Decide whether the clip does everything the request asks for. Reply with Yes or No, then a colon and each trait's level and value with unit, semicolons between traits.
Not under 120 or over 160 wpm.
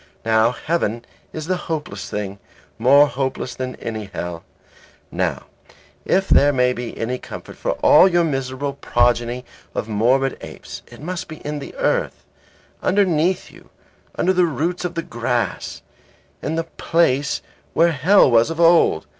Yes: average, 145 wpm